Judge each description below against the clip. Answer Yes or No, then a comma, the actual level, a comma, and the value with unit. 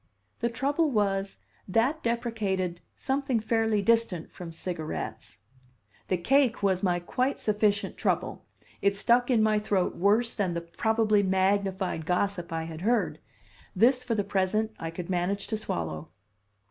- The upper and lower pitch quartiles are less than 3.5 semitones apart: No, average, 4.1 semitones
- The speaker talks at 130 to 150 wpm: Yes, average, 145 wpm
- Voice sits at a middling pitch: No, high, 200 Hz